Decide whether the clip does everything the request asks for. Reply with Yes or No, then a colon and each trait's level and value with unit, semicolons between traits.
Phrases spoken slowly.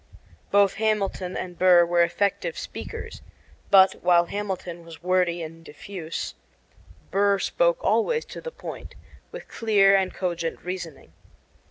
Yes: slow, 130 wpm